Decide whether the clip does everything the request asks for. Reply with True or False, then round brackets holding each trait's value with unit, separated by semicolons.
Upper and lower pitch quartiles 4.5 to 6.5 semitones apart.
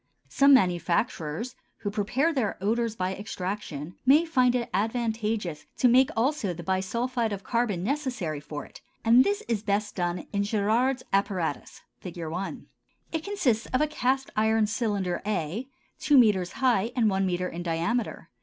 True (5.2 semitones)